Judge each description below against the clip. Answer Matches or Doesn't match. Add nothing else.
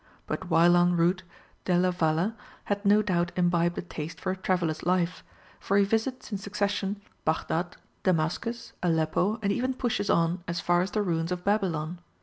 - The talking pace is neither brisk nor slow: Matches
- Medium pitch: Matches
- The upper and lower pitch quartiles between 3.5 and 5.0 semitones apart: Doesn't match